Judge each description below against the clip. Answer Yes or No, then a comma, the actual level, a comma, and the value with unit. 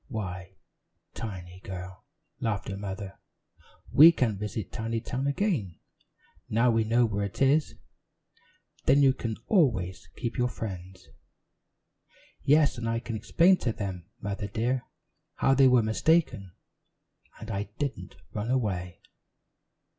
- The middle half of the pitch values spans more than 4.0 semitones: Yes, average, 4.9 semitones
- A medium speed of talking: No, slow, 125 wpm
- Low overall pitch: Yes, low, 110 Hz